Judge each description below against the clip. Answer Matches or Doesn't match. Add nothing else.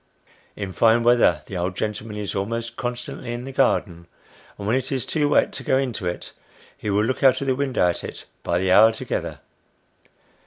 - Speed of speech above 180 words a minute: Matches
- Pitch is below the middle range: Matches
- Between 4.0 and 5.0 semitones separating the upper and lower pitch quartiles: Matches